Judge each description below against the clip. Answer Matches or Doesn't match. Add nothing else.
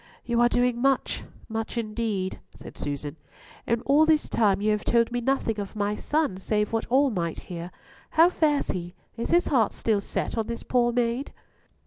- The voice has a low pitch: Doesn't match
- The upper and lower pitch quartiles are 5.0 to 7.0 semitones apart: Doesn't match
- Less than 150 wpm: Doesn't match